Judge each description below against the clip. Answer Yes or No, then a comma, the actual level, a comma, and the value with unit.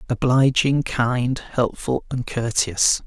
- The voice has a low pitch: Yes, low, 125 Hz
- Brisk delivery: No, slow, 100 wpm